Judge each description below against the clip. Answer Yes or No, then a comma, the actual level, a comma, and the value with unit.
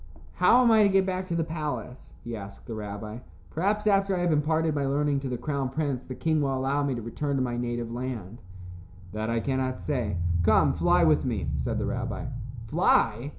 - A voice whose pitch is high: No, low, 135 Hz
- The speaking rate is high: Yes, fast, 210 wpm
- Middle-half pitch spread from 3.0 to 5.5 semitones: Yes, average, 5.1 semitones